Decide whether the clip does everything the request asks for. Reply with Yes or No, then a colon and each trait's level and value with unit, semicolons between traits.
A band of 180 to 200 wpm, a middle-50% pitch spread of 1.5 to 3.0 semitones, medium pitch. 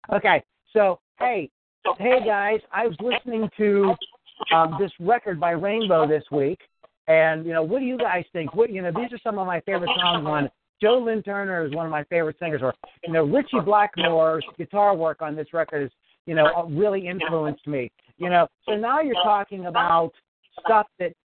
No: average, 195 wpm; average, 4.6 semitones; medium, 175 Hz